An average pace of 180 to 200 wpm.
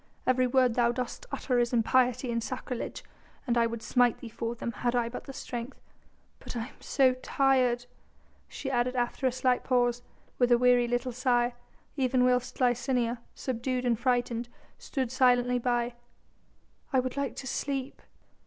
No: average, 165 wpm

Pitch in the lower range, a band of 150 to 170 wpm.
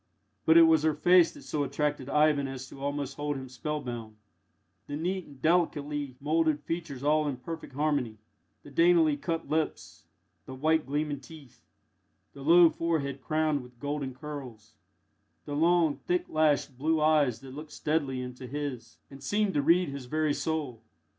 No: medium, 145 Hz; average, 165 wpm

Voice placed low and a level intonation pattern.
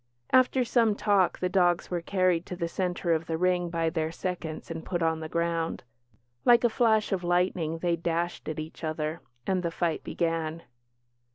No: medium, 170 Hz; narrow, 2.0 semitones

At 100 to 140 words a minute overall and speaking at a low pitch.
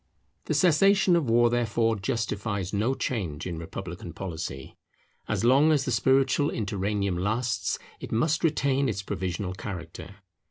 Yes: slow, 135 wpm; low, 110 Hz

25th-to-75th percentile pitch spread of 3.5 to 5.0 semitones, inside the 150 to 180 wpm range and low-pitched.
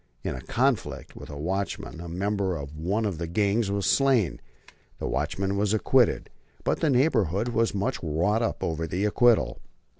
Yes: average, 4.3 semitones; average, 175 wpm; low, 100 Hz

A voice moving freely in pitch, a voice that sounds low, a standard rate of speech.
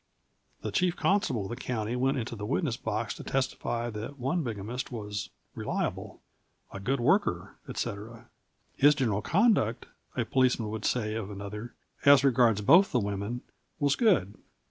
No: average, 4.3 semitones; low, 120 Hz; average, 155 wpm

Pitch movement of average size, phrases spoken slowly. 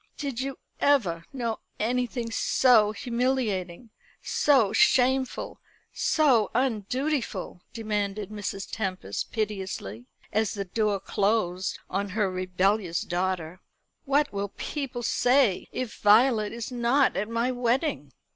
Yes: average, 4.4 semitones; slow, 110 wpm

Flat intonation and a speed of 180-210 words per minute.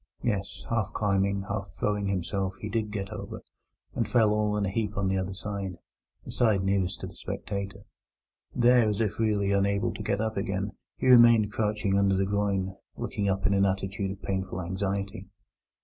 Yes: narrow, 1.5 semitones; average, 185 wpm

